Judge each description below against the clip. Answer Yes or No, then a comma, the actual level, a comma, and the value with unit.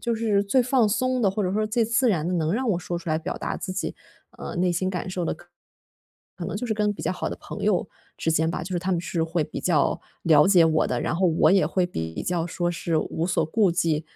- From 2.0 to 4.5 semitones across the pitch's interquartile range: Yes, average, 4.1 semitones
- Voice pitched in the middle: Yes, medium, 180 Hz